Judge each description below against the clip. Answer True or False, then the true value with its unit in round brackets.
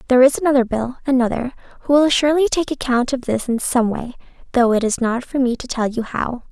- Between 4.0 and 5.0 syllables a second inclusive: False (6.0 syllables/s)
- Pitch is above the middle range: True (250 Hz)